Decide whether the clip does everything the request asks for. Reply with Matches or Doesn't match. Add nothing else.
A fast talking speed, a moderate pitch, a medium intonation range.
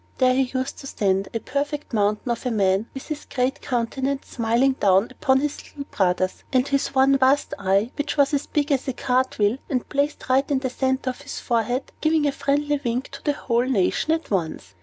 Doesn't match